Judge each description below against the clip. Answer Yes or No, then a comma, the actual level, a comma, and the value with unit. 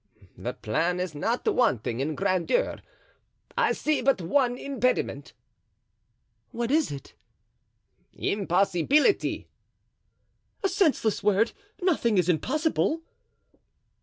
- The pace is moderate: No, slow, 95 wpm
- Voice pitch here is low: No, high, 230 Hz